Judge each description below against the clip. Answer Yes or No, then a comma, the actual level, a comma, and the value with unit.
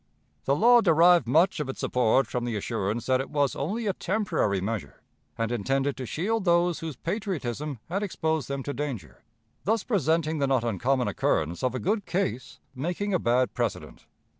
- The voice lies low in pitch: No, medium, 145 Hz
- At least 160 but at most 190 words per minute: Yes, average, 180 wpm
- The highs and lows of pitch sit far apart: Yes, wide, 6.4 semitones